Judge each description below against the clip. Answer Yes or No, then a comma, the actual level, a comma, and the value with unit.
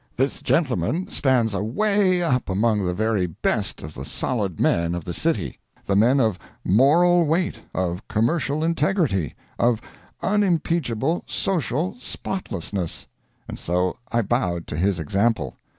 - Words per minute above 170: No, slow, 135 wpm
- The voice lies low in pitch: Yes, low, 115 Hz